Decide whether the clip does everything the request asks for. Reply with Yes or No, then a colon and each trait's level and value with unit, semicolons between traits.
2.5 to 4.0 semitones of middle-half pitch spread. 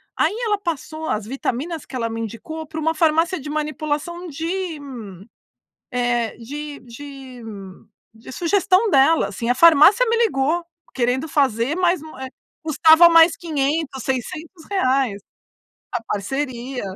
No: average, 4.7 semitones